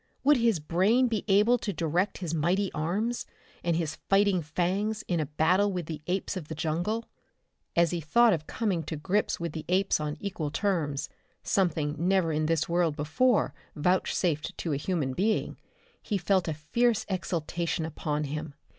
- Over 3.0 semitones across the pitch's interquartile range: Yes, average, 4.3 semitones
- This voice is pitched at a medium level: Yes, medium, 175 Hz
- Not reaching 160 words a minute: No, average, 170 wpm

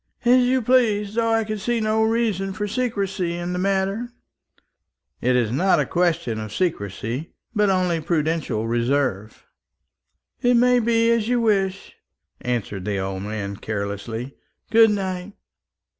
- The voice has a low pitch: No, high, 190 Hz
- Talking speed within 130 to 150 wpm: Yes, average, 145 wpm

